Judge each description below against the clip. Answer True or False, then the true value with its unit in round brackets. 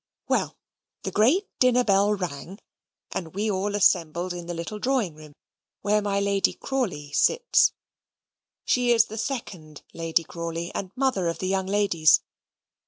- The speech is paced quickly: False (150 wpm)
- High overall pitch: True (195 Hz)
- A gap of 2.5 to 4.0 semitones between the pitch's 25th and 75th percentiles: False (4.4 semitones)